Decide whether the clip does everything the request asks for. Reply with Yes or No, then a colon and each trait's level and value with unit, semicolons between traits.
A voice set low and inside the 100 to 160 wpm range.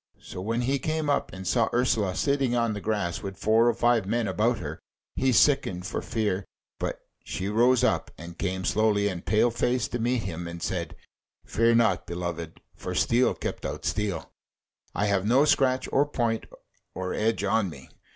No: low, 110 Hz; average, 185 wpm